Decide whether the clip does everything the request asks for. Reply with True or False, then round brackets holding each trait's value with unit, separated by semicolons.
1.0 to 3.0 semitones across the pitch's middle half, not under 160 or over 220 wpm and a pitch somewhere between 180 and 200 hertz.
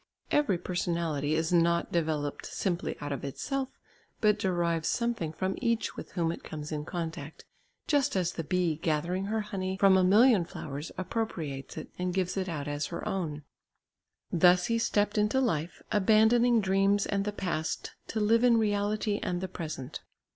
False (4.3 semitones; 170 wpm; 185 Hz)